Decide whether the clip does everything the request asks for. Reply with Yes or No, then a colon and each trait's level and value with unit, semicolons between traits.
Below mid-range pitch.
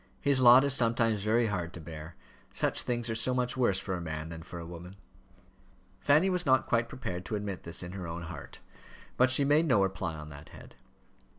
Yes: low, 105 Hz